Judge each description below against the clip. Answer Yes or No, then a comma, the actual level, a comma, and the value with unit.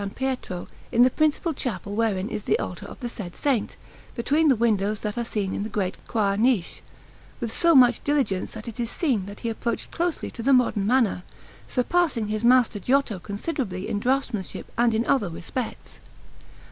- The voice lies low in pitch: No, high, 230 Hz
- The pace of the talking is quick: No, average, 180 wpm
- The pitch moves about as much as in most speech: Yes, average, 4.3 semitones